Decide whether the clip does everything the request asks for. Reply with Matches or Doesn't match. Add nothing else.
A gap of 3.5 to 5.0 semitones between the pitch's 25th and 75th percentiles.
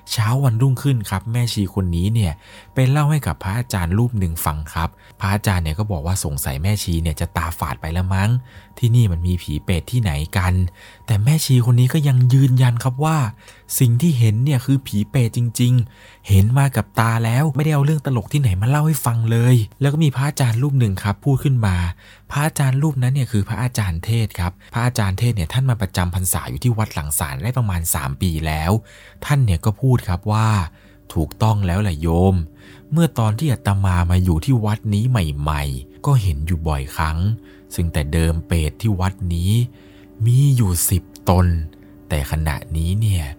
Doesn't match